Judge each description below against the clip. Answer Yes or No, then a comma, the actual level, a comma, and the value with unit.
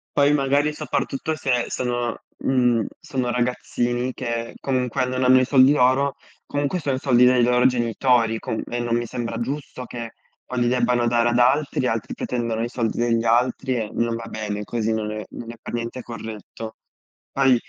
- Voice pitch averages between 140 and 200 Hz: No, low, 120 Hz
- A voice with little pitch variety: Yes, narrow, 1.8 semitones